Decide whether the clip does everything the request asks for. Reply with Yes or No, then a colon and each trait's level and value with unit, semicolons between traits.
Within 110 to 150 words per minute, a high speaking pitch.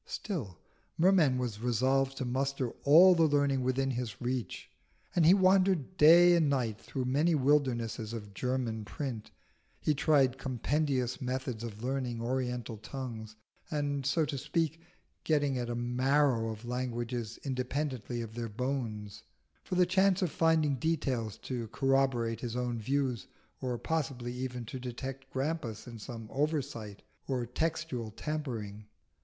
No: average, 140 wpm; low, 130 Hz